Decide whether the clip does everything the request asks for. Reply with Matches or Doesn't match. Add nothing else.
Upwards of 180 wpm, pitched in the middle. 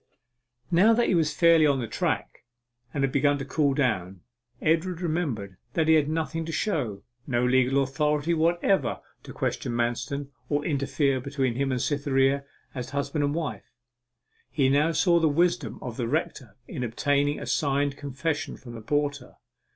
Doesn't match